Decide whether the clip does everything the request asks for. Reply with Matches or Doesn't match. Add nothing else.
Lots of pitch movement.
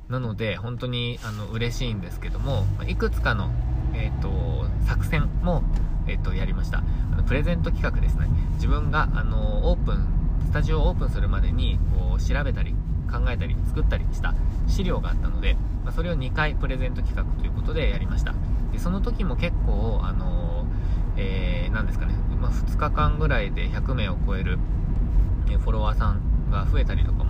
Doesn't match